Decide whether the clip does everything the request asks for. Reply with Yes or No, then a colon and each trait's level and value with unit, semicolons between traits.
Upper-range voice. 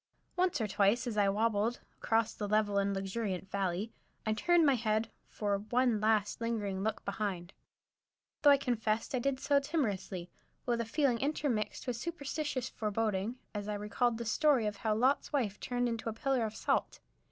Yes: high, 225 Hz